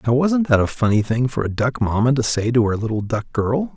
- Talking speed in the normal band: No, fast, 270 wpm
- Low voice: Yes, low, 120 Hz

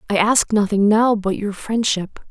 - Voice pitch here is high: Yes, high, 210 Hz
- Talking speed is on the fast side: No, average, 185 wpm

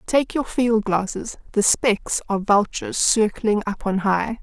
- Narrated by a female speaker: Yes, female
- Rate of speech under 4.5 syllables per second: Yes, 4.2 syllables/s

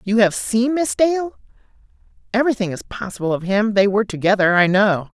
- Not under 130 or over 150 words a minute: No, average, 175 wpm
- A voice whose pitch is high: Yes, high, 215 Hz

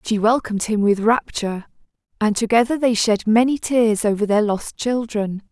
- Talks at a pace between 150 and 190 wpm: Yes, average, 165 wpm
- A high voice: Yes, high, 220 Hz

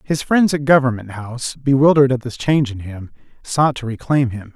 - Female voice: No, male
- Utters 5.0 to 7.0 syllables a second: Yes, 5.5 syllables/s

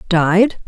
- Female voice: Yes, female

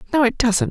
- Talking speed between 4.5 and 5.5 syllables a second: No, 6.0 syllables/s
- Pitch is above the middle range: Yes, very high, 255 Hz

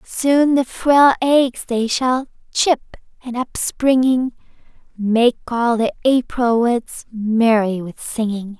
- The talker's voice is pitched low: No, high, 240 Hz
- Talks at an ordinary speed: No, slow, 120 wpm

